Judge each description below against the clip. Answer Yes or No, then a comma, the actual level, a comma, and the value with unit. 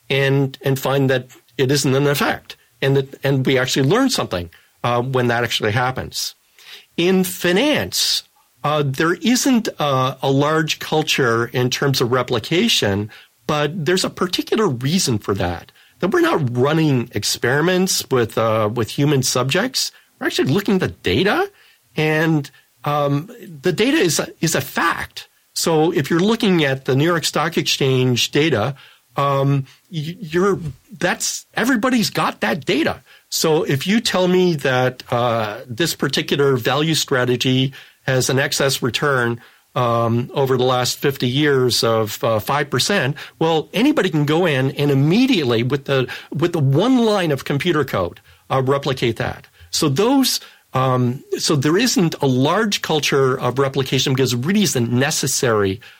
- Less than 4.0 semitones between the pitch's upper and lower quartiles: No, average, 4.8 semitones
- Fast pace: No, average, 160 wpm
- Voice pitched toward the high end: No, medium, 140 Hz